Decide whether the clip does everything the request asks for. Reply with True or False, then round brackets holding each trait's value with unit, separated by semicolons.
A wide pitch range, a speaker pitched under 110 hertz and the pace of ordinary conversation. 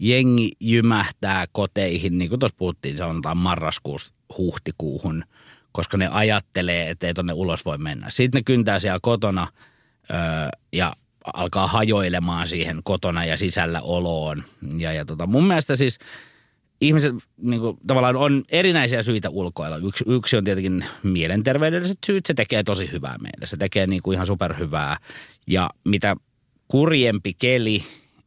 True (5.9 semitones; 100 Hz; 140 wpm)